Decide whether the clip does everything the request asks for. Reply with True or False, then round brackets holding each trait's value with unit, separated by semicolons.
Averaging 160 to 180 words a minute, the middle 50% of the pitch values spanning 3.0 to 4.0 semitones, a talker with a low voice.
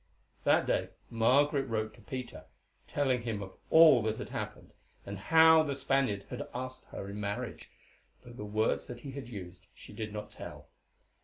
False (170 wpm; 4.5 semitones; 115 Hz)